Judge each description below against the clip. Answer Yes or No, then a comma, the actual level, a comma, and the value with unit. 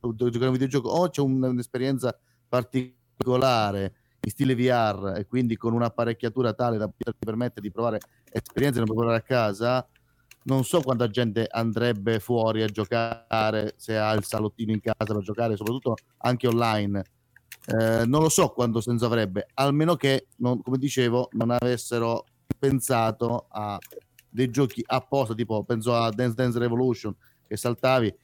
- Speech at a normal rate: Yes, average, 150 wpm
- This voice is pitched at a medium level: No, low, 120 Hz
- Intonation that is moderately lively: No, narrow, 2.2 semitones